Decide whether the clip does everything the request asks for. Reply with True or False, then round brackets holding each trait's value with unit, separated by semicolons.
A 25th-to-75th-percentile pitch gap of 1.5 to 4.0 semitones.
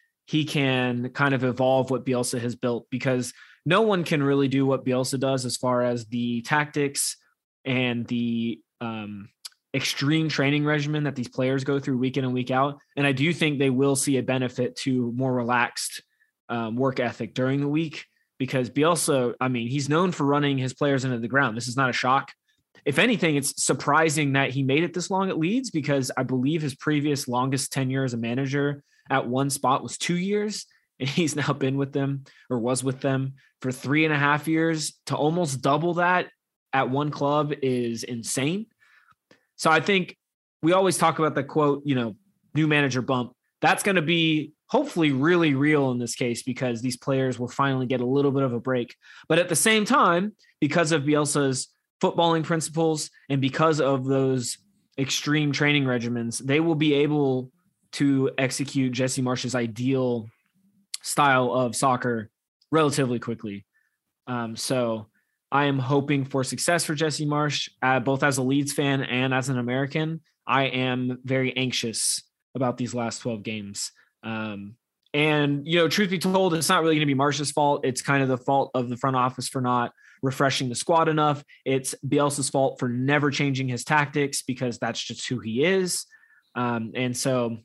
True (3.1 semitones)